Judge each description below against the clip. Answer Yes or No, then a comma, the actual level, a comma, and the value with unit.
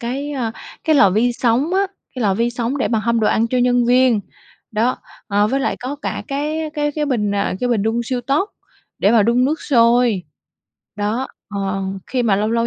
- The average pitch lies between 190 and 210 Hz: No, high, 240 Hz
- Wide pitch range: No, average, 3.4 semitones